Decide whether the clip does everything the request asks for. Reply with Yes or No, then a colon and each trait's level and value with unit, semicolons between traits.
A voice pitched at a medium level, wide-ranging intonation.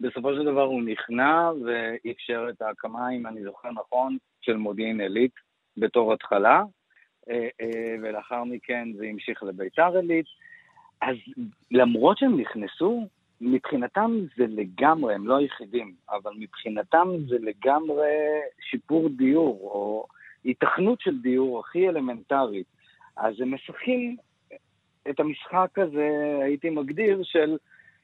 No: low, 130 Hz; wide, 6.0 semitones